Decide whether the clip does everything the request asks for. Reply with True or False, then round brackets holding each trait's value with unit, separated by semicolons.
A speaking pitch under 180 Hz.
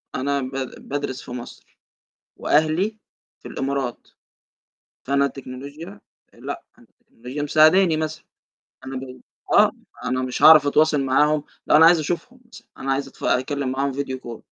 True (140 Hz)